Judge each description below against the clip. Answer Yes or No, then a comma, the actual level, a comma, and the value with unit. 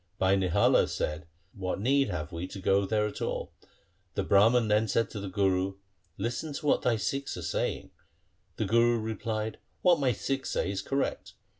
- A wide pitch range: No, average, 3.9 semitones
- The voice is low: Yes, low, 105 Hz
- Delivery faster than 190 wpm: Yes, average, 200 wpm